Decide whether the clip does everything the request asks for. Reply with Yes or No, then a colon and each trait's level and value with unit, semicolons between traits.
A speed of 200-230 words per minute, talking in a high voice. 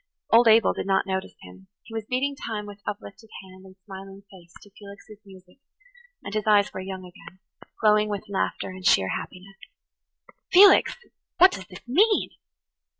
No: average, 165 wpm; high, 200 Hz